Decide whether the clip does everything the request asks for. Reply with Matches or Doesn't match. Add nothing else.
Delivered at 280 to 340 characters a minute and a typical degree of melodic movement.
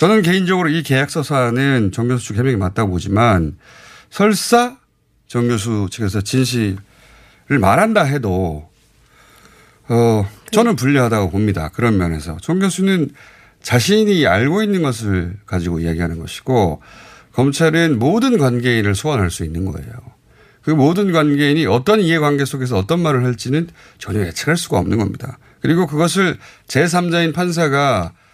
Doesn't match